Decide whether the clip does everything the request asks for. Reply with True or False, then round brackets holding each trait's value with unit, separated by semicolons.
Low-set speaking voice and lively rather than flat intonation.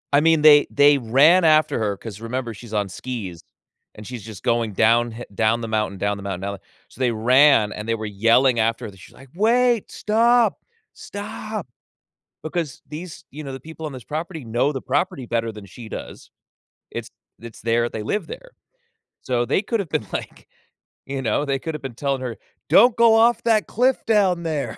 True (130 Hz; 6.4 semitones)